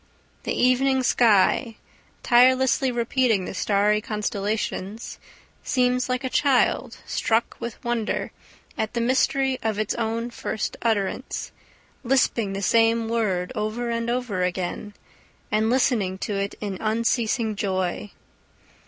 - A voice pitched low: No, high, 225 Hz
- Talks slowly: Yes, slow, 120 wpm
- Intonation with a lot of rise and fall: No, average, 3.1 semitones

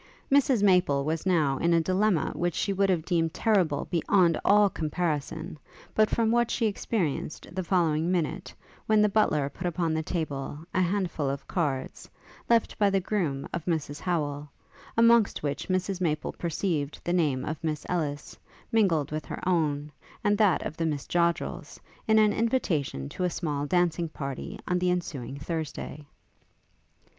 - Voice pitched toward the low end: No, medium, 170 Hz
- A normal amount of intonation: Yes, average, 4.2 semitones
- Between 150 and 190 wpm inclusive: Yes, average, 165 wpm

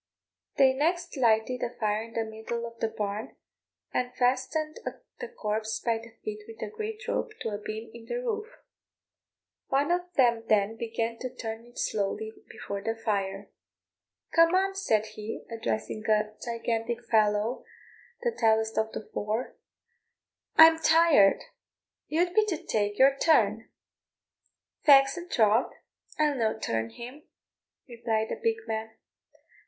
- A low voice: No, high, 230 Hz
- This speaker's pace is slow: No, average, 145 wpm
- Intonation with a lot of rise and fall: Yes, wide, 5.8 semitones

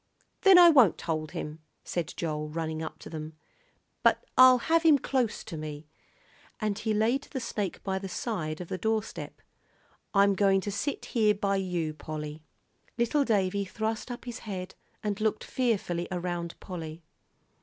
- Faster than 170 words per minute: No, average, 165 wpm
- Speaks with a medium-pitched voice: No, high, 195 Hz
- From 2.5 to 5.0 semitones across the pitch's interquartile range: No, wide, 5.4 semitones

